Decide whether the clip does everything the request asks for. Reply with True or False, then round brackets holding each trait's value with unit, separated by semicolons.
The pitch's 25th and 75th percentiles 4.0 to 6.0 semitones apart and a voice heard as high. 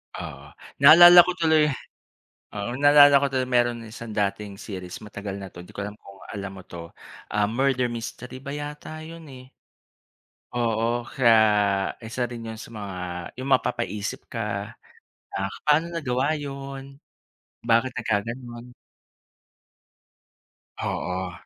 False (4.8 semitones; 120 Hz)